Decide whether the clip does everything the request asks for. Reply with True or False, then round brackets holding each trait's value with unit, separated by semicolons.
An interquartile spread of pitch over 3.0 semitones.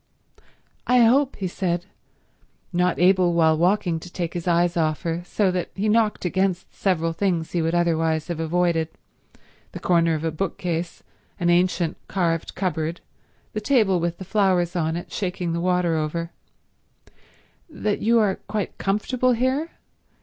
False (2.7 semitones)